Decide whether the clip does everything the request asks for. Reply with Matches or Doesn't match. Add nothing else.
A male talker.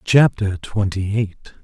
Matches